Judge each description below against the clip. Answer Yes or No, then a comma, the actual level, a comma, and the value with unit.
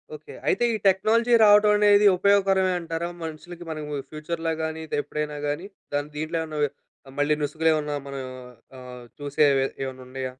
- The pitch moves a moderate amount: Yes, average, 3.9 semitones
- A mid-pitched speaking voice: Yes, medium, 155 Hz